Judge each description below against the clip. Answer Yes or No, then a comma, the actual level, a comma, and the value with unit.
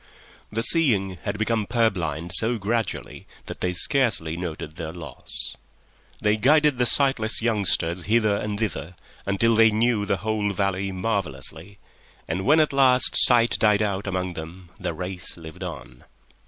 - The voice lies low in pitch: Yes, low, 100 Hz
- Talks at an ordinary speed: Yes, average, 150 wpm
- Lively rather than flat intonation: No, average, 4.1 semitones